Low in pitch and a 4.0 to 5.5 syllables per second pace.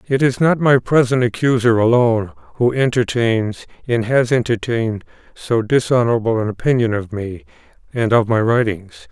Yes: low, 120 Hz; 5.0 syllables/s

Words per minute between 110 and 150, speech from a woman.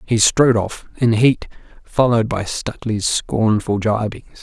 No: slow, 135 wpm; male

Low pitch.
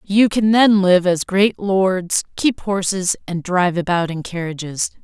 No: medium, 185 Hz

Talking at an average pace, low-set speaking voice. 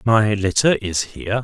Yes: average, 165 wpm; low, 105 Hz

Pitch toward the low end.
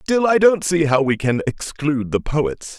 No: medium, 150 Hz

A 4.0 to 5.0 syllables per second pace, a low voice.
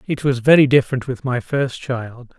Yes: 4.9 syllables/s; low, 130 Hz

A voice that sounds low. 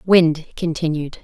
No: medium, 160 Hz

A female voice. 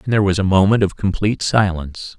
No: male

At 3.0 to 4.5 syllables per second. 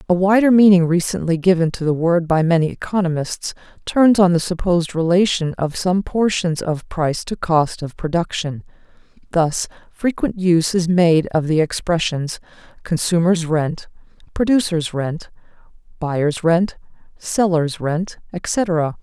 Yes: 4.4 syllables/s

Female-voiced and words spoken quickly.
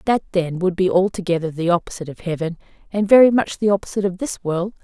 Yes: female; fast, 210 wpm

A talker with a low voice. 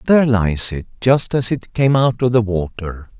Yes: low, 115 Hz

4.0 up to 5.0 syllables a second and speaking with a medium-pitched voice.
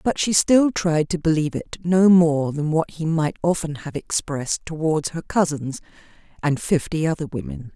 Yes: 4.8 syllables/s; medium, 155 Hz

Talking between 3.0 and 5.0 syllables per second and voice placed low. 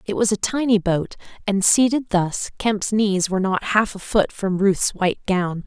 No: 4.5 syllables/s; high, 200 Hz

